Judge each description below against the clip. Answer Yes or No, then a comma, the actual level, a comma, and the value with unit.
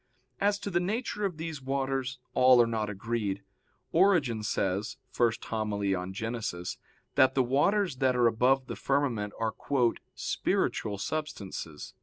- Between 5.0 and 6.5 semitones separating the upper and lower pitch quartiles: Yes, average, 5.3 semitones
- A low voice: Yes, low, 125 Hz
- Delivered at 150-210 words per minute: No, average, 140 wpm